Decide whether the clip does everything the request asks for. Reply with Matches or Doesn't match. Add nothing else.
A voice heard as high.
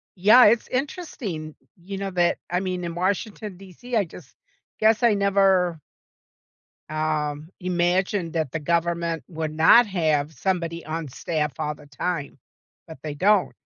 Doesn't match